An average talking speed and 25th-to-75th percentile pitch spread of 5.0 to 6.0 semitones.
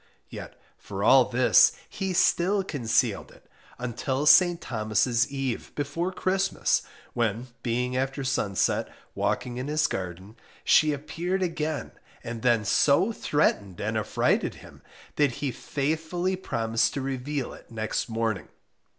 No: slow, 130 wpm; wide, 5.5 semitones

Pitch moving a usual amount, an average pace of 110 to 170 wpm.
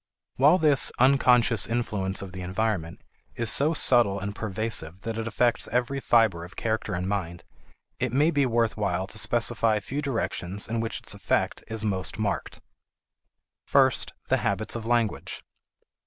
Yes: average, 3.7 semitones; average, 160 wpm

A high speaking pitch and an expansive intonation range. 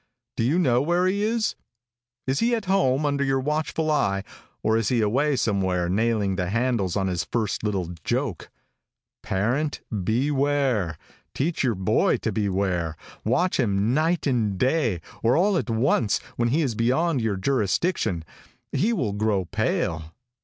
No: low, 120 Hz; wide, 6.8 semitones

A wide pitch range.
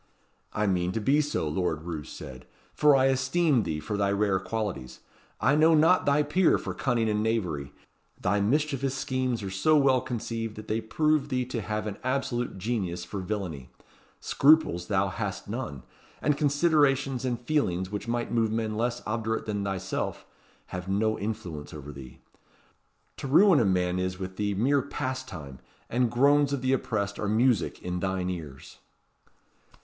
Yes: wide, 5.9 semitones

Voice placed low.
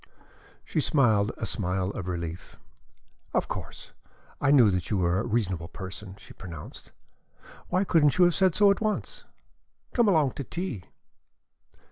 Yes: low, 110 Hz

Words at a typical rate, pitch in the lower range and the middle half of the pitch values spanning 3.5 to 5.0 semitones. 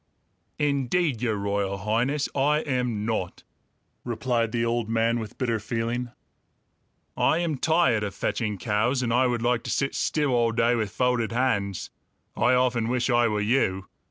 No: average, 160 wpm; low, 120 Hz; narrow, 2.6 semitones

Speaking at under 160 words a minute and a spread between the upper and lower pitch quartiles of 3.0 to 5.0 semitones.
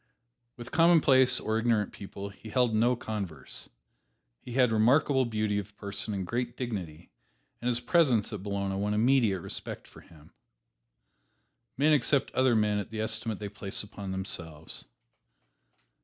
Yes: average, 145 wpm; average, 3.6 semitones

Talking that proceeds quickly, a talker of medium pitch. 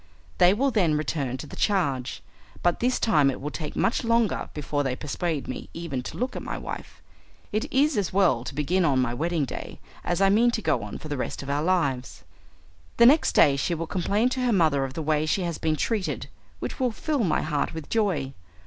Yes: fast, 225 wpm; medium, 165 Hz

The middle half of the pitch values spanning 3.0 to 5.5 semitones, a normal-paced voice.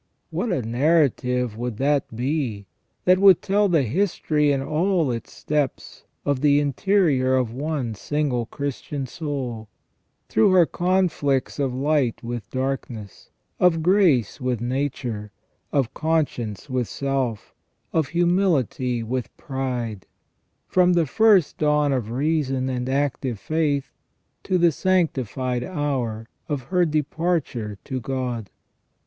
No: average, 4.5 semitones; slow, 125 wpm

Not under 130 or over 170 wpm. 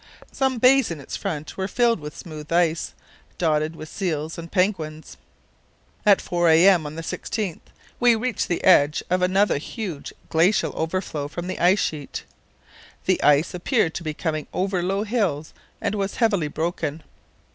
Yes: average, 160 wpm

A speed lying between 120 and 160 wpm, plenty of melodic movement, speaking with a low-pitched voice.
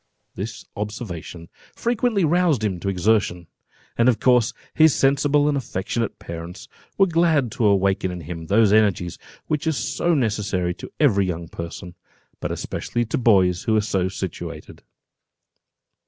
Yes: average, 145 wpm; wide, 7.0 semitones; low, 105 Hz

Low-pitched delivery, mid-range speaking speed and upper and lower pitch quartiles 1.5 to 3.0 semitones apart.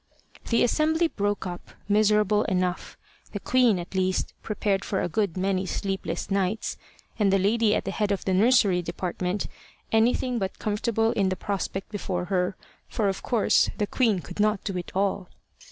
No: high, 200 Hz; average, 170 wpm; narrow, 2.5 semitones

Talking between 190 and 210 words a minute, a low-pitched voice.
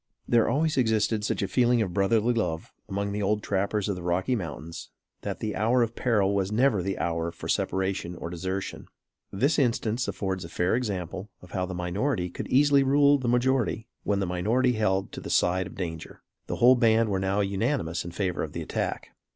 Yes: average, 200 wpm; low, 100 Hz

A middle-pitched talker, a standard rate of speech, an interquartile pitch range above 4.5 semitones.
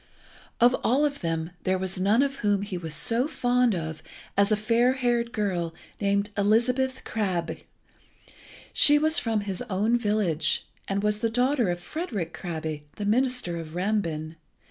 No: high, 210 Hz; average, 160 wpm; wide, 5.5 semitones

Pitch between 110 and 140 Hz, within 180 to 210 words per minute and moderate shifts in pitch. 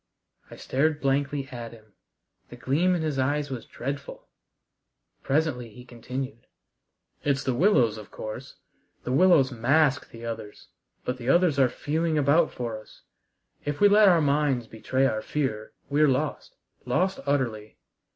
No: low, 135 Hz; average, 150 wpm; average, 3.8 semitones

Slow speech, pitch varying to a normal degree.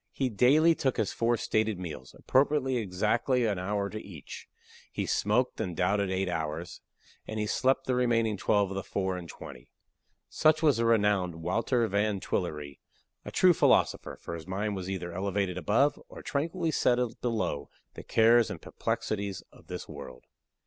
No: average, 170 wpm; average, 4.8 semitones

